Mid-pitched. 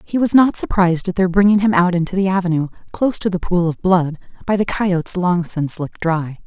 Yes: medium, 180 Hz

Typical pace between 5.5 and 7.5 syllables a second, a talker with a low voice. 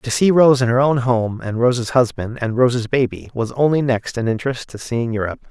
Yes: 5.6 syllables/s; low, 125 Hz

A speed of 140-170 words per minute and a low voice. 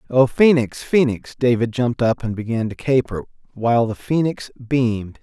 Yes: average, 160 wpm; low, 120 Hz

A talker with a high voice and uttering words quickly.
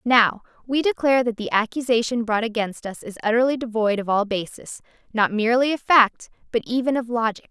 No: high, 235 Hz; average, 185 wpm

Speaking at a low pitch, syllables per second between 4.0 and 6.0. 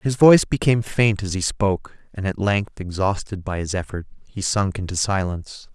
Yes: low, 100 Hz; 5.5 syllables/s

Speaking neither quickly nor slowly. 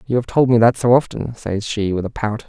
No: fast, 290 wpm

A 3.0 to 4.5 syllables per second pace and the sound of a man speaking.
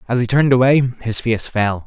No: 5.3 syllables/s; male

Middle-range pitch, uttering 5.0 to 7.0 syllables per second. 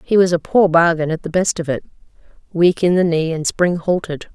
Yes: medium, 170 Hz; 5.3 syllables/s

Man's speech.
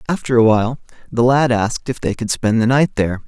Yes: male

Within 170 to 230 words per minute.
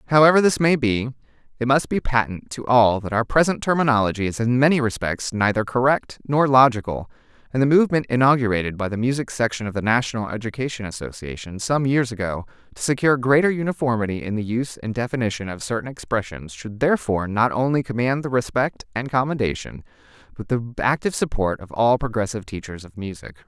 Yes: average, 175 wpm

